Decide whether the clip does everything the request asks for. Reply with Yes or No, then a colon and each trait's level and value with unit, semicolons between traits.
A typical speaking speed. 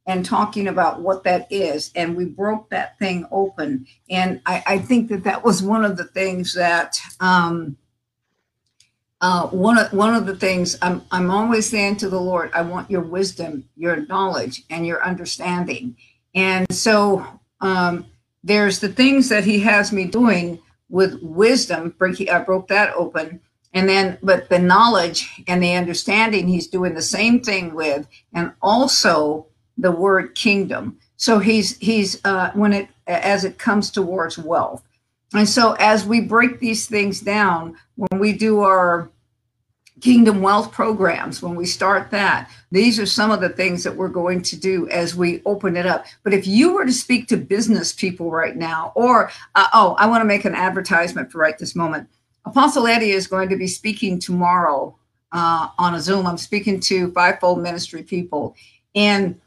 Yes: average, 175 wpm